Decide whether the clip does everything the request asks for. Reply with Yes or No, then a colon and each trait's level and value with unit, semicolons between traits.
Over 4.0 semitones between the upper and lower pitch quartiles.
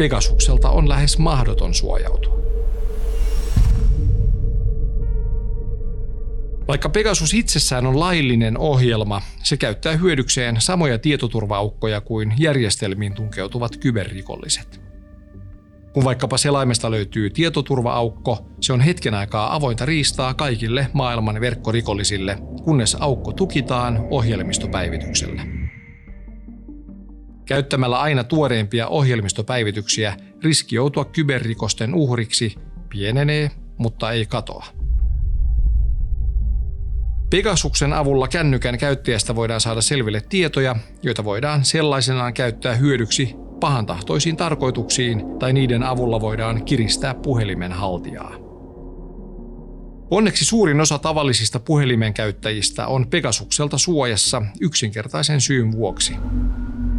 Yes: wide, 5.5 semitones